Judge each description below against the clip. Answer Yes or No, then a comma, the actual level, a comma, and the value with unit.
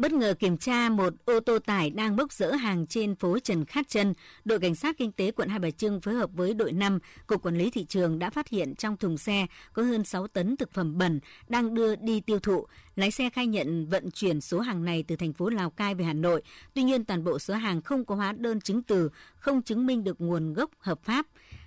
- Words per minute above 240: Yes, fast, 250 wpm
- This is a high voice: Yes, high, 200 Hz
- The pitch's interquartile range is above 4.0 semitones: Yes, average, 4.5 semitones